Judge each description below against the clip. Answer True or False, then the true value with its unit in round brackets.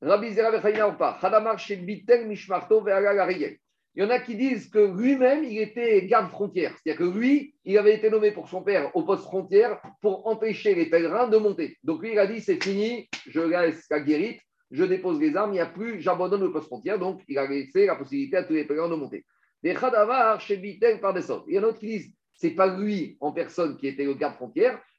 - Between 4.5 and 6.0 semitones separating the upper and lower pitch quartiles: True (4.9 semitones)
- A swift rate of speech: False (210 wpm)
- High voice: True (210 Hz)